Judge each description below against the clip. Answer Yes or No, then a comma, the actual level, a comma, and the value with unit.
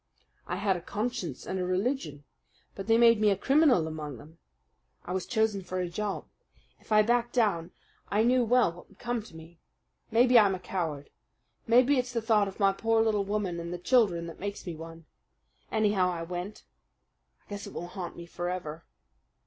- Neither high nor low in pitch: No, high, 195 Hz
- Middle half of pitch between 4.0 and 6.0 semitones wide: Yes, average, 4.7 semitones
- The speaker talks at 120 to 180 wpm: No, average, 195 wpm